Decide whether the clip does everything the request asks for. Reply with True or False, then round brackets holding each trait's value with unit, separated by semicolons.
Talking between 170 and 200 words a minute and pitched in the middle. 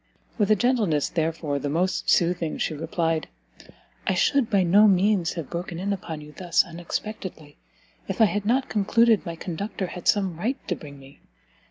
True (175 wpm; 180 Hz)